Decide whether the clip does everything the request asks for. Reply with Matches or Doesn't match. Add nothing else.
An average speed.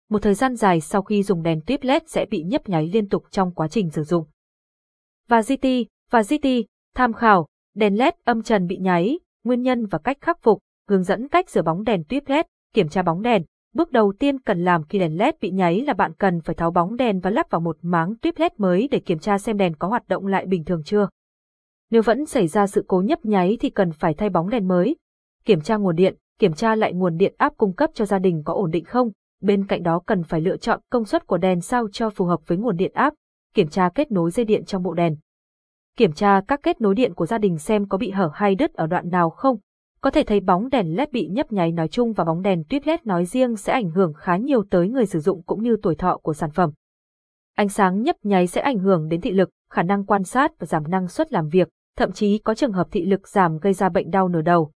Doesn't match